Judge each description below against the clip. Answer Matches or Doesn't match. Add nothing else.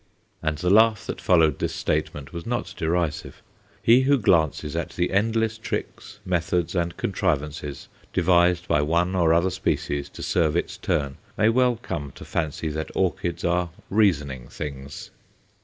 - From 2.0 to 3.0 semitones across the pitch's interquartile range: Doesn't match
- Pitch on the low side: Matches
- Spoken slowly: Doesn't match